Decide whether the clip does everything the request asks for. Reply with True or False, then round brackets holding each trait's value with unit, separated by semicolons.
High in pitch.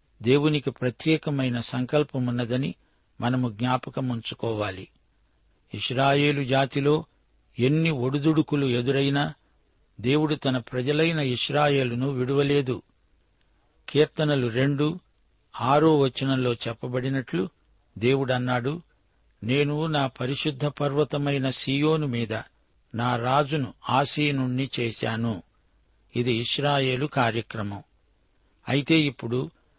False (130 Hz)